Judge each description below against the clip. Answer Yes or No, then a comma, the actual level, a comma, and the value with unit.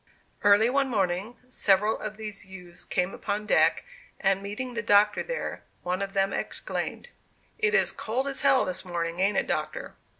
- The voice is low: No, high, 205 Hz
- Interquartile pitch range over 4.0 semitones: No, average, 3.3 semitones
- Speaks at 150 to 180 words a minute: Yes, average, 170 wpm